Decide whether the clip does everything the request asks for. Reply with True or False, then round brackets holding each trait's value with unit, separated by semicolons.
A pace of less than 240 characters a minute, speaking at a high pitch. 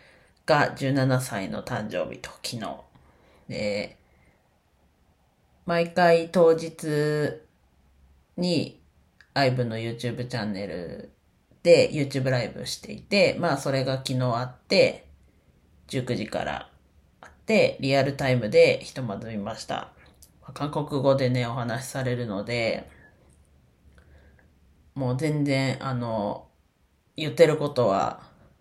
False (215 characters per minute; 120 Hz)